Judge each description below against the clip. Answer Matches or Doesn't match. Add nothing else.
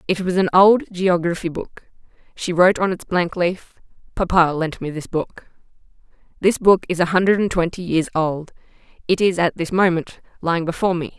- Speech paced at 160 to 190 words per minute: Matches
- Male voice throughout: Doesn't match